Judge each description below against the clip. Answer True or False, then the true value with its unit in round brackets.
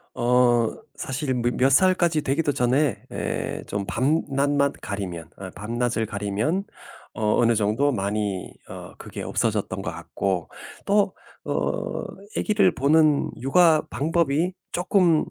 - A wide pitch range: True (6.2 semitones)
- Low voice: True (130 Hz)